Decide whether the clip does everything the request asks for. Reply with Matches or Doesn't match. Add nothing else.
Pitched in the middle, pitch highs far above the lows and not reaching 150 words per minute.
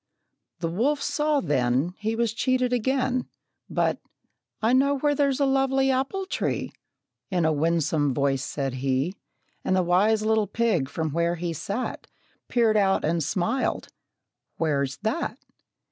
Doesn't match